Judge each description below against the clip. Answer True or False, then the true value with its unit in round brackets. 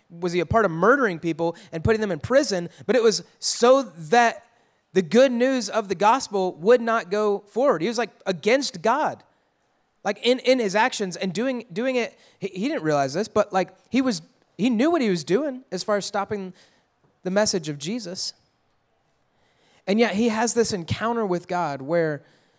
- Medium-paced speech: True (190 wpm)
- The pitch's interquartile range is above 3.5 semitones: True (4.7 semitones)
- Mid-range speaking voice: False (210 Hz)